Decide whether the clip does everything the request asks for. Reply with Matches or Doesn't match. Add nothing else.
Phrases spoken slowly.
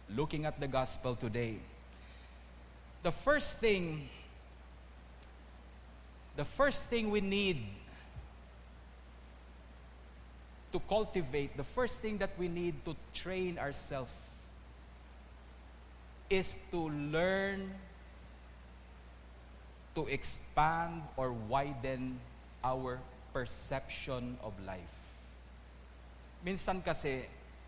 Matches